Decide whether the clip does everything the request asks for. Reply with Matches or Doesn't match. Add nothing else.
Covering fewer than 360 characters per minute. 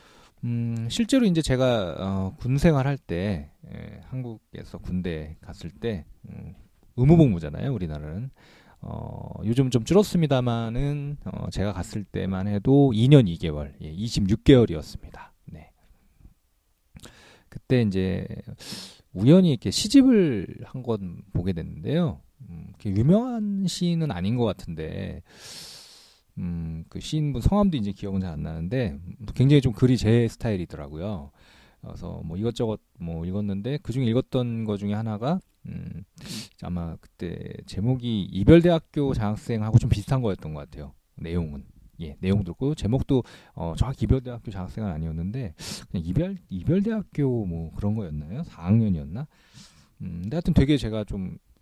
Matches